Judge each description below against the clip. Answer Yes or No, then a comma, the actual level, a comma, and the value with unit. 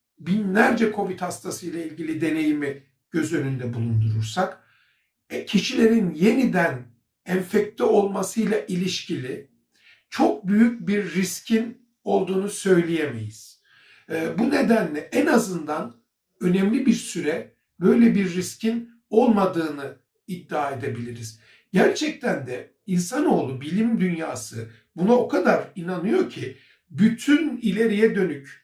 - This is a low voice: No, medium, 185 Hz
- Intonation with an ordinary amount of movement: No, wide, 6.1 semitones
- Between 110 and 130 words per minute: No, slow, 95 wpm